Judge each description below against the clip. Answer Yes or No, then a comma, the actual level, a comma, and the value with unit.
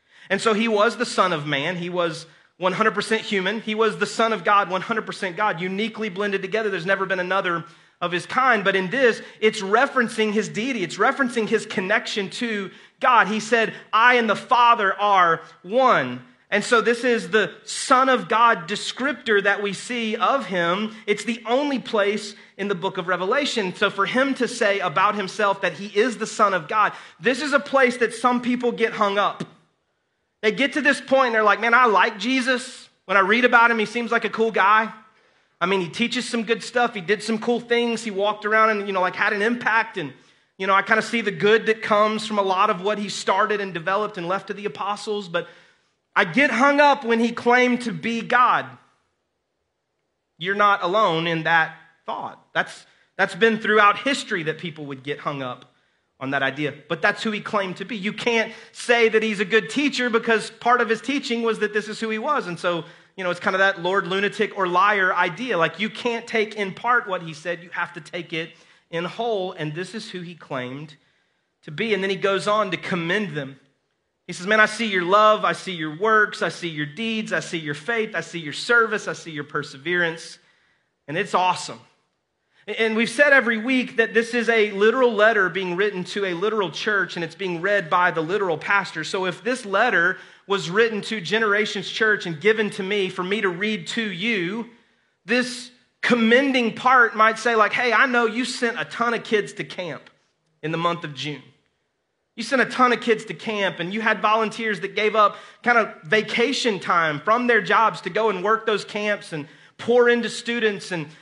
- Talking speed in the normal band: No, fast, 215 wpm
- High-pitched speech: Yes, high, 210 Hz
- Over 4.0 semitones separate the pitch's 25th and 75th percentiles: No, average, 3.6 semitones